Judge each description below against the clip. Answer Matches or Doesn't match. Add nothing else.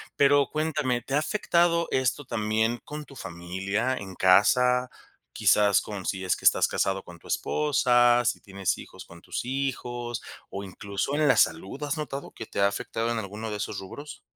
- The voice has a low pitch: Matches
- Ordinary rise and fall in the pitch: Doesn't match